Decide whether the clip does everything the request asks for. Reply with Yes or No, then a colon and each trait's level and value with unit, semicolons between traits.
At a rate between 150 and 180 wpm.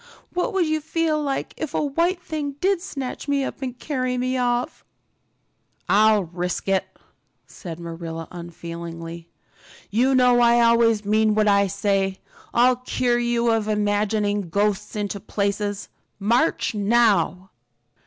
No: slow, 135 wpm